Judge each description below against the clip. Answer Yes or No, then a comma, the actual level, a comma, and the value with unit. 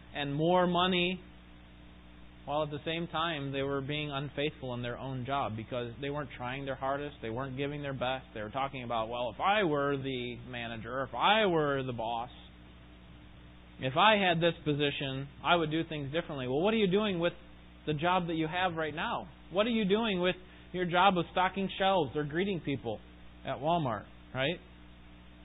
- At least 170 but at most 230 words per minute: Yes, average, 190 wpm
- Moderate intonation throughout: No, wide, 6.5 semitones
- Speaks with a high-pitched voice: No, medium, 140 Hz